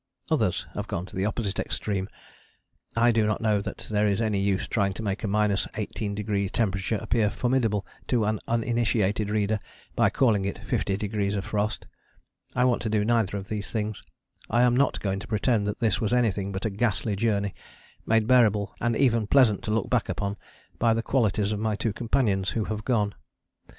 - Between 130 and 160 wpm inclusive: No, average, 195 wpm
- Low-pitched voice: Yes, low, 105 Hz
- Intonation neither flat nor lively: No, narrow, 2.2 semitones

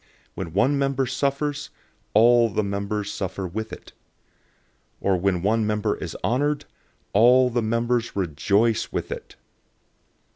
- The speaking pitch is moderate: No, low, 110 Hz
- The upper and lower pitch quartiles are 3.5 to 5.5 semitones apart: Yes, average, 3.8 semitones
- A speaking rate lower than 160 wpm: Yes, slow, 135 wpm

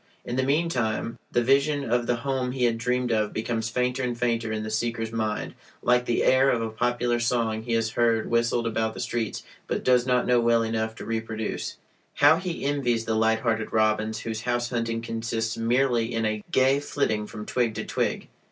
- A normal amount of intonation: No, narrow, 1.7 semitones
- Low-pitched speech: Yes, low, 115 Hz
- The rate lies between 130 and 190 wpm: No, average, 200 wpm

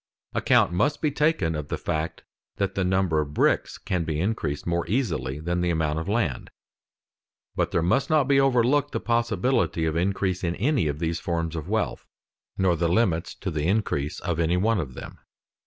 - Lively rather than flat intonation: Yes, wide, 5.7 semitones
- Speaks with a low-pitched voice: Yes, very low, 90 Hz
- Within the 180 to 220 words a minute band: Yes, average, 190 wpm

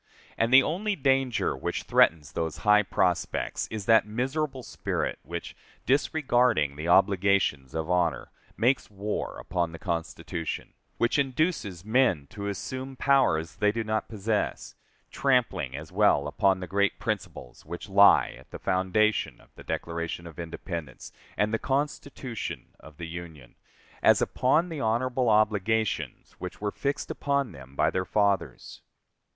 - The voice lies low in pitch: Yes, low, 105 Hz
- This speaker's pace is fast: No, average, 145 wpm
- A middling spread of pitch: No, wide, 6.9 semitones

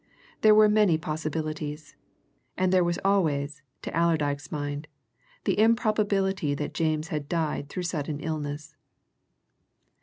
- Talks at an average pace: No, slow, 120 wpm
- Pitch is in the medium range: Yes, medium, 155 Hz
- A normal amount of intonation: Yes, average, 4.0 semitones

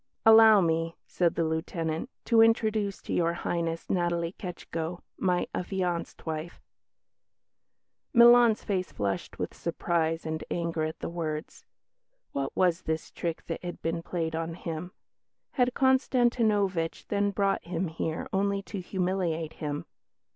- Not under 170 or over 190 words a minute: No, slow, 135 wpm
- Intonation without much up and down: No, average, 3.5 semitones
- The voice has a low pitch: No, medium, 175 Hz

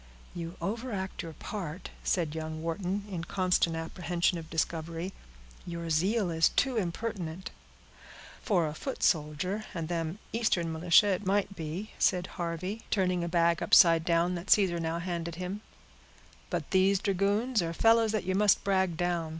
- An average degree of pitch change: Yes, average, 3.1 semitones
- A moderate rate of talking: Yes, average, 155 wpm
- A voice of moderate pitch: Yes, medium, 180 Hz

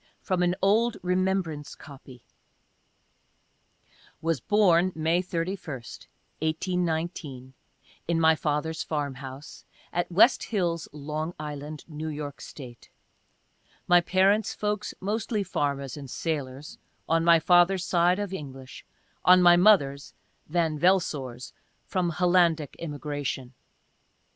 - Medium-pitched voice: Yes, medium, 165 Hz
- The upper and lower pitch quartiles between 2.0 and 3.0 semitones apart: No, average, 3.9 semitones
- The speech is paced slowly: Yes, slow, 120 wpm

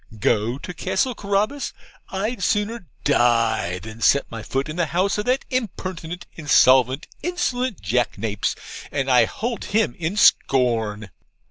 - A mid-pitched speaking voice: Yes, medium, 165 Hz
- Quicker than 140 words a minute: No, slow, 135 wpm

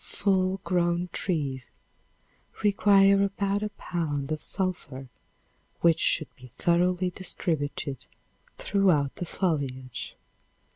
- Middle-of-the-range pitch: Yes, medium, 175 Hz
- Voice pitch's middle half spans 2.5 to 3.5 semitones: No, average, 5.2 semitones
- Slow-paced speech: Yes, slow, 95 wpm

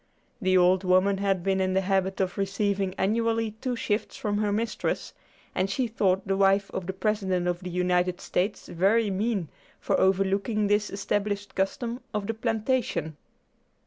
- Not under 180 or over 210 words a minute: No, average, 165 wpm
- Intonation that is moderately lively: No, narrow, 2.2 semitones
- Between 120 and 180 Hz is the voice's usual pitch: No, high, 195 Hz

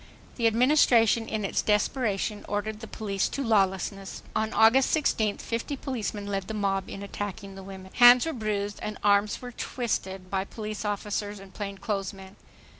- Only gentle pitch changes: Yes, narrow, 2.2 semitones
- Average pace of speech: Yes, average, 160 wpm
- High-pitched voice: Yes, high, 210 Hz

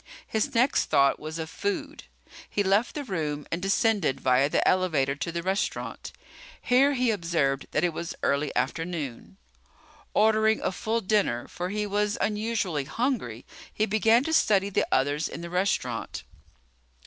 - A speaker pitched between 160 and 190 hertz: Yes, medium, 185 Hz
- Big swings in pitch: Yes, wide, 6.6 semitones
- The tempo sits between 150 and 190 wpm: Yes, average, 155 wpm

